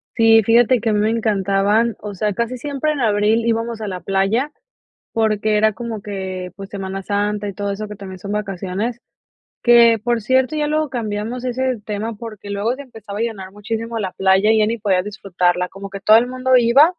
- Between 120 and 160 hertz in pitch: No, high, 215 Hz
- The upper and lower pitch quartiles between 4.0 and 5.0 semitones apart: No, average, 2.8 semitones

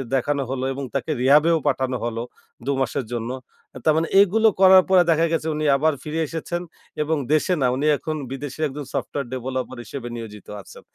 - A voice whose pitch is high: No, medium, 140 Hz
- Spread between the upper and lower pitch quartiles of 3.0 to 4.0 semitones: Yes, average, 3.7 semitones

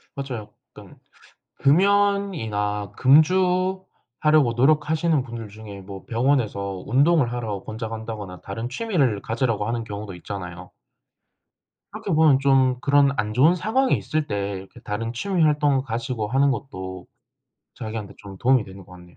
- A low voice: Yes, low, 120 Hz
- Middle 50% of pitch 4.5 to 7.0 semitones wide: Yes, wide, 6.2 semitones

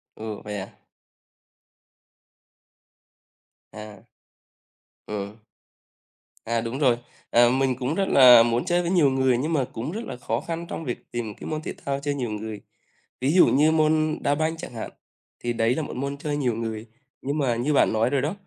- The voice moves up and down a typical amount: Yes, average, 4.7 semitones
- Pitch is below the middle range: Yes, low, 130 Hz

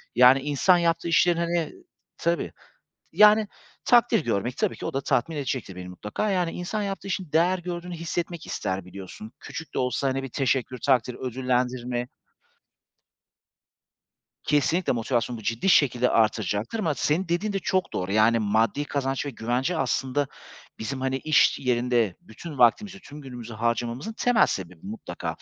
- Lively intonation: Yes, wide, 6.5 semitones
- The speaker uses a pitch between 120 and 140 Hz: Yes, low, 135 Hz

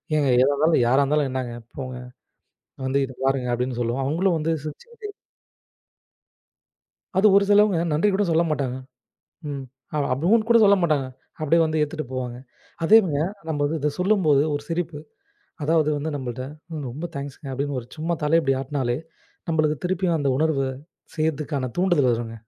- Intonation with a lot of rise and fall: No, average, 4.0 semitones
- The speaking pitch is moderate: Yes, medium, 150 Hz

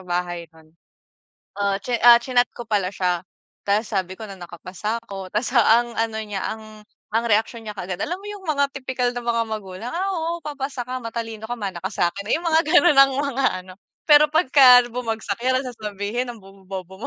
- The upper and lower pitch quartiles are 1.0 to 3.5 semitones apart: No, average, 4.7 semitones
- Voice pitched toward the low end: No, high, 225 Hz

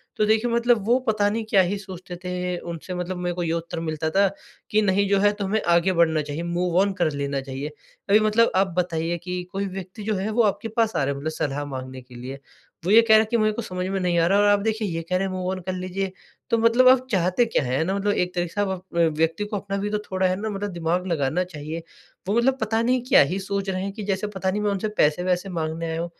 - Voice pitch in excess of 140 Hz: Yes, medium, 185 Hz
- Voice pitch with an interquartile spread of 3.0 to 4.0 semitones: Yes, average, 3.5 semitones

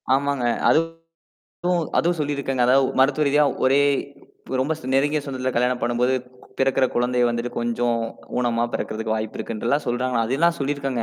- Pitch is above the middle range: No, low, 130 Hz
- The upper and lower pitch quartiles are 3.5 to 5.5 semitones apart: No, average, 2.8 semitones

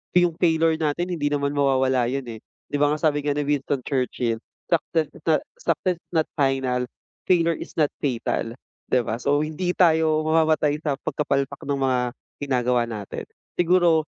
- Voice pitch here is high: No, medium, 145 Hz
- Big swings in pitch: No, average, 3.4 semitones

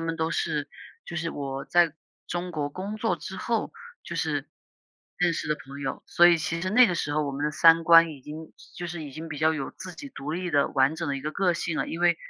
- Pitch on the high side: No, medium, 160 Hz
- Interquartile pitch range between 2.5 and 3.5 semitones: Yes, average, 2.9 semitones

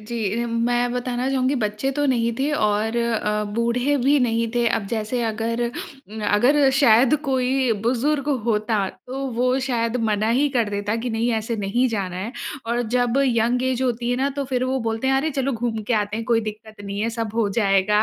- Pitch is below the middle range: No, high, 235 Hz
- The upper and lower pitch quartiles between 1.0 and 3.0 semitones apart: Yes, average, 2.7 semitones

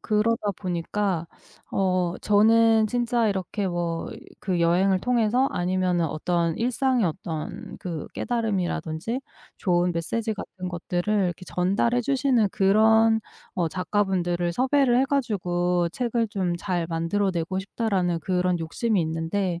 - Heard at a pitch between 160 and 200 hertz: Yes, high, 190 Hz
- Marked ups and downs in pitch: No, average, 4.2 semitones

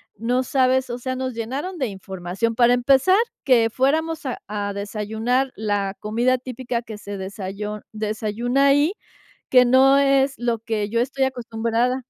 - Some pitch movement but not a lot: Yes, average, 3.5 semitones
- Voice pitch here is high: Yes, high, 240 Hz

